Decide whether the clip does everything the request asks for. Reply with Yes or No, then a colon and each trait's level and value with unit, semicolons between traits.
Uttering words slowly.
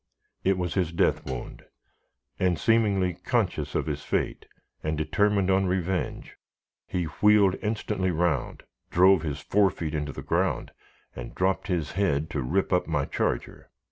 No: average, 150 wpm